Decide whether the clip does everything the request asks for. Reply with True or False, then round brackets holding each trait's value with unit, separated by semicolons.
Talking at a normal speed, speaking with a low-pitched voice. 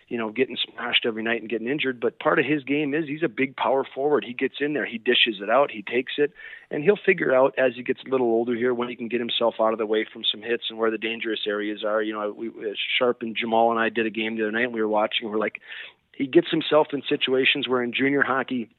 False (285 wpm; 120 Hz)